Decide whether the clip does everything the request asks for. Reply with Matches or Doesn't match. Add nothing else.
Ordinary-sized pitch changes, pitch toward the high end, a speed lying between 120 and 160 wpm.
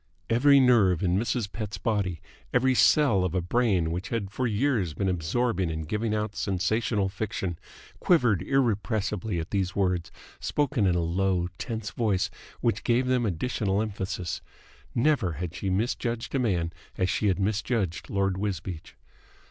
Doesn't match